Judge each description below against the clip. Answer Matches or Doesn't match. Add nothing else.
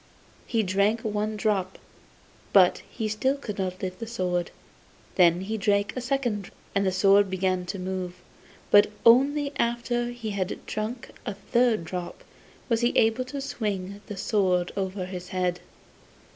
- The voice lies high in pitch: Matches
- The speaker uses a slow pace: Doesn't match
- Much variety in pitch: Doesn't match